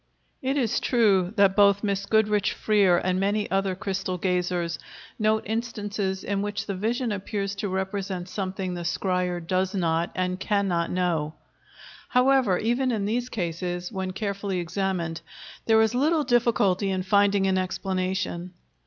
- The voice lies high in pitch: Yes, high, 195 Hz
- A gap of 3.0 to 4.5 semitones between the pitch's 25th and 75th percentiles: No, narrow, 2.5 semitones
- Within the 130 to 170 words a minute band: Yes, average, 150 wpm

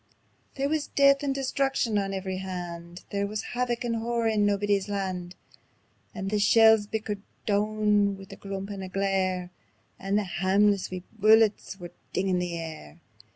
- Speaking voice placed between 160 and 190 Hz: No, high, 200 Hz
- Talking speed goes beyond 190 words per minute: No, average, 160 wpm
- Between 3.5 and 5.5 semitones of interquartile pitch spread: No, average, 2.7 semitones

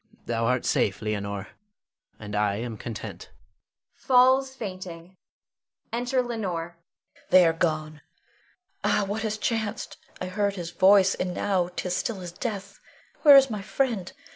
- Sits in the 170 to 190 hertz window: Yes, medium, 185 Hz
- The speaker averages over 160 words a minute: No, average, 140 wpm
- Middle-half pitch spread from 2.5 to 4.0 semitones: No, wide, 5.4 semitones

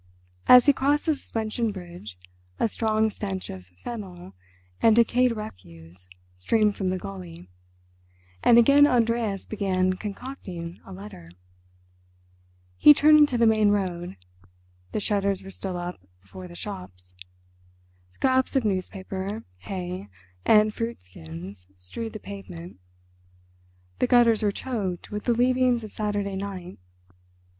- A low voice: No, high, 200 Hz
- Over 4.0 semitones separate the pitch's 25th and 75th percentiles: Yes, average, 4.6 semitones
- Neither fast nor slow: No, slow, 130 wpm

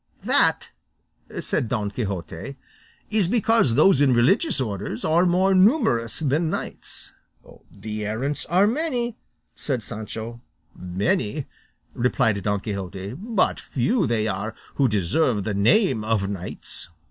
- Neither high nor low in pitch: No, low, 120 Hz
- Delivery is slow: Yes, slow, 120 wpm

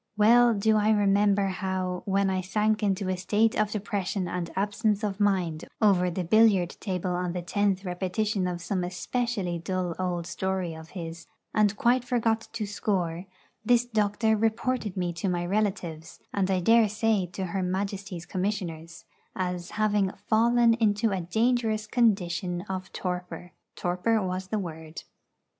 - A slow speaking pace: No, average, 155 wpm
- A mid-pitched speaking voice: No, high, 195 Hz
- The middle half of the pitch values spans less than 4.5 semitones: Yes, average, 3.0 semitones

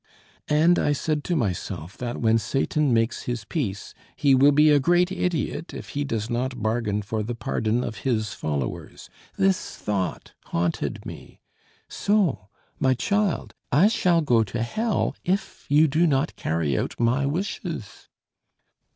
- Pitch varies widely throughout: Yes, wide, 6.5 semitones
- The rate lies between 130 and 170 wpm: Yes, average, 150 wpm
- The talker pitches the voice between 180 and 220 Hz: No, low, 130 Hz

